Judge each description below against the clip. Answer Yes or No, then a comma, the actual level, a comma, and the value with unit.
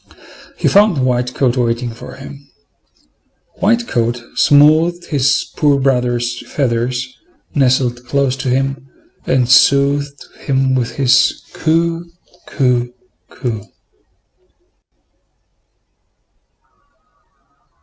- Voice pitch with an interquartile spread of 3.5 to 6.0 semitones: No, narrow, 2.6 semitones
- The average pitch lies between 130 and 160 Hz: Yes, low, 135 Hz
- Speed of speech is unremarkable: No, slow, 90 wpm